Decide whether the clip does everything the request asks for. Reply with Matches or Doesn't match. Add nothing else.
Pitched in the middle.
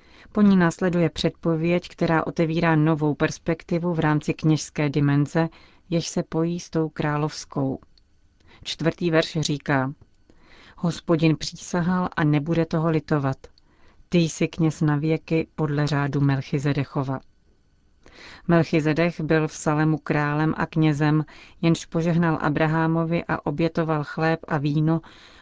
Matches